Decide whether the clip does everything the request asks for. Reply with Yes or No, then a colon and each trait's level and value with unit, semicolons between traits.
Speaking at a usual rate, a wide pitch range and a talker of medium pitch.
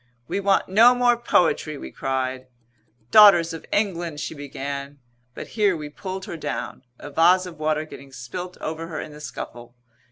No: average, 170 wpm; average, 4.8 semitones; medium, 160 Hz